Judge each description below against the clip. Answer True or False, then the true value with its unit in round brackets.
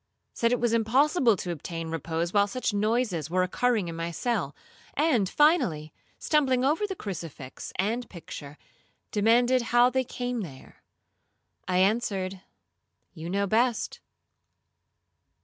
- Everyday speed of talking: False (130 wpm)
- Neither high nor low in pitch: False (215 Hz)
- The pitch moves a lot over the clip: True (6.2 semitones)